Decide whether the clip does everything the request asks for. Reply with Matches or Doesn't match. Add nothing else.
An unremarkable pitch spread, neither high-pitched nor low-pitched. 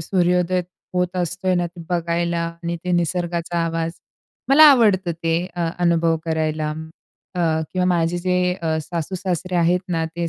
Doesn't match